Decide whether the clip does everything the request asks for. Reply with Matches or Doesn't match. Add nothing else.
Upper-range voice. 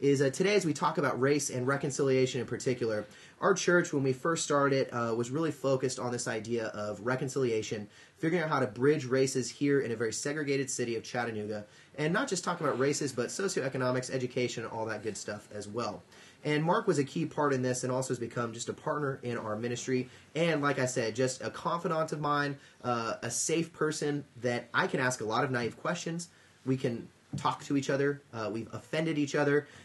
Doesn't match